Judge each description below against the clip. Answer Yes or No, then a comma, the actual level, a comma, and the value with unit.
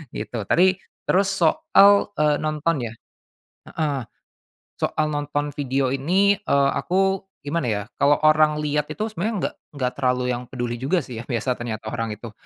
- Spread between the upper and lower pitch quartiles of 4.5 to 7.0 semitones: Yes, average, 5.0 semitones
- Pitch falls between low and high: Yes, medium, 145 Hz